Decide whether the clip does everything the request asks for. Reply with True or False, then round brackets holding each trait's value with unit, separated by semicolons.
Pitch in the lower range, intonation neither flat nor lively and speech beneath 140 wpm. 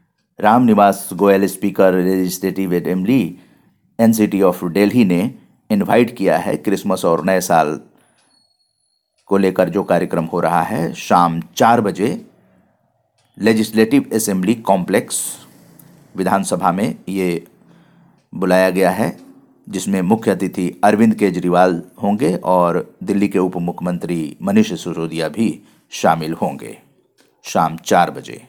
False (95 Hz; 2.3 semitones; 120 wpm)